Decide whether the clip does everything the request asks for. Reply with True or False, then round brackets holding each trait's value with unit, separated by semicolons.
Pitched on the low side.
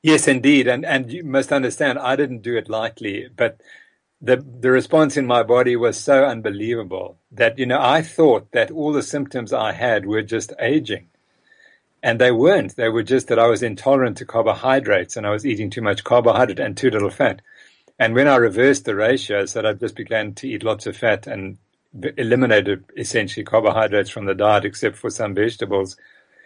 True (125 Hz)